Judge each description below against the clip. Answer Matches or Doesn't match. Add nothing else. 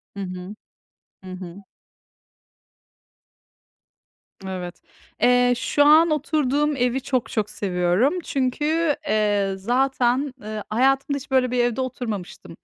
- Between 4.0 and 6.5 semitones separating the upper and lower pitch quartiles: Matches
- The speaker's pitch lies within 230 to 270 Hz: Matches